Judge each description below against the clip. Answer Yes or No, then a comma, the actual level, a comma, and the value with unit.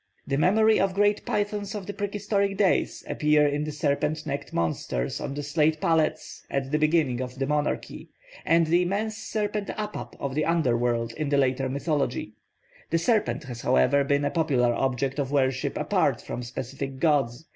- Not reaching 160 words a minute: No, average, 175 wpm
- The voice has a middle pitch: Yes, medium, 150 Hz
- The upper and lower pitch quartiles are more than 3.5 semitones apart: Yes, average, 5.1 semitones